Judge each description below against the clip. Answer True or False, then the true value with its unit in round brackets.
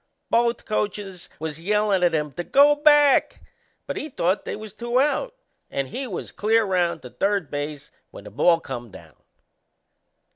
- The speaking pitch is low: False (195 Hz)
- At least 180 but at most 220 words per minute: False (170 wpm)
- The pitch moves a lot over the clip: True (6.8 semitones)